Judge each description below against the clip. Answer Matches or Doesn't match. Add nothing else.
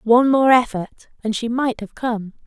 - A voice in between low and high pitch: Doesn't match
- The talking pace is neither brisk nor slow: Matches